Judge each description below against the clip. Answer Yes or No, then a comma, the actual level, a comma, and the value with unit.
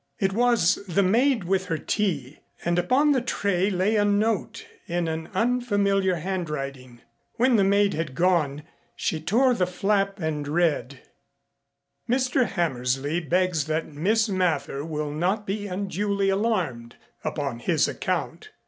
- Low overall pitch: No, medium, 185 Hz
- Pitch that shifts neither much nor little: Yes, average, 4.8 semitones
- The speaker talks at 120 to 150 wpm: Yes, average, 140 wpm